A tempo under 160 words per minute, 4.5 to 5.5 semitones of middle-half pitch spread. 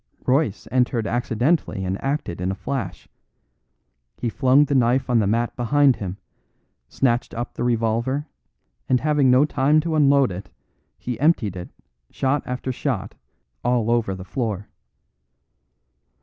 No: slow, 135 wpm; average, 4.1 semitones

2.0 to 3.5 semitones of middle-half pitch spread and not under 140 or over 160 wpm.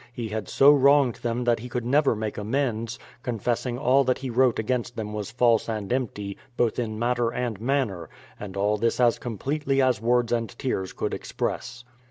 No: narrow, 2.6 semitones; average, 195 wpm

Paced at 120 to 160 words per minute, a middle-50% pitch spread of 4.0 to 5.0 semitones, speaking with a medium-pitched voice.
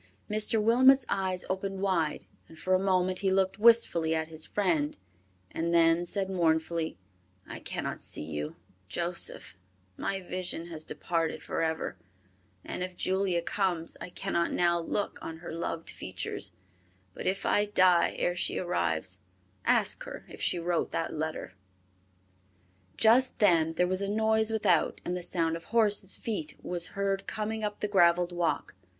No: average, 155 wpm; average, 3.1 semitones; medium, 180 Hz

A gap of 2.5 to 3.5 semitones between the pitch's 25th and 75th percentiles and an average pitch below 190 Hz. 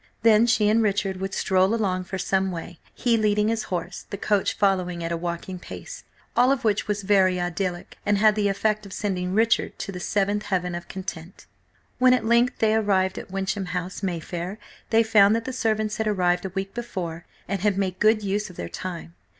No: average, 2.8 semitones; high, 195 Hz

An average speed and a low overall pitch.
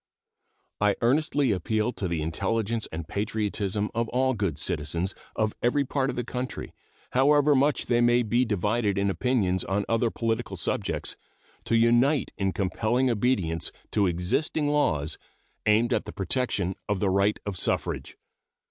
Yes: average, 150 wpm; low, 110 Hz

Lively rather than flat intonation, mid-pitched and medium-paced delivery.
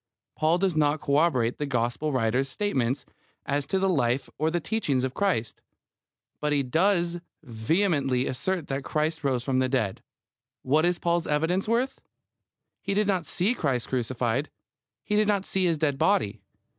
Yes: wide, 5.7 semitones; medium, 150 Hz; average, 165 wpm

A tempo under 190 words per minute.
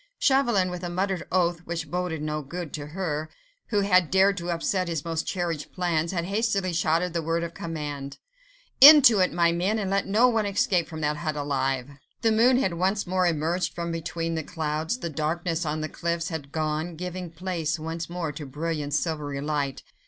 No: average, 195 wpm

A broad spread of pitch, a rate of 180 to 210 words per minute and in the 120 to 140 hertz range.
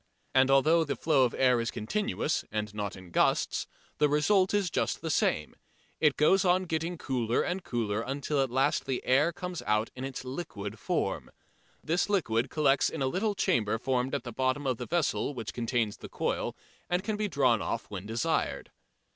Yes: wide, 6.0 semitones; average, 190 wpm; low, 135 Hz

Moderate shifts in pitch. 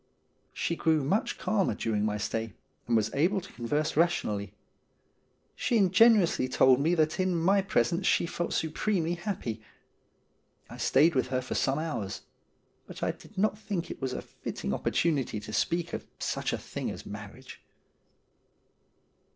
No: wide, 6.9 semitones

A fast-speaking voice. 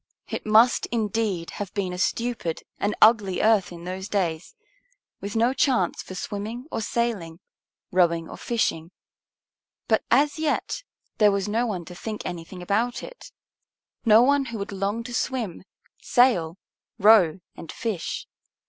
No: average, 150 wpm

